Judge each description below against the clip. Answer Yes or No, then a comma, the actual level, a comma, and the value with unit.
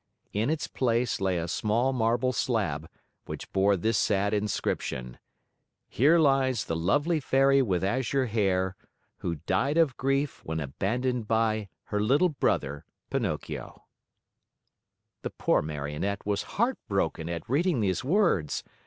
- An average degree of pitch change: No, wide, 6.2 semitones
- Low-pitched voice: Yes, low, 110 Hz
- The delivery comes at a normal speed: No, slow, 130 wpm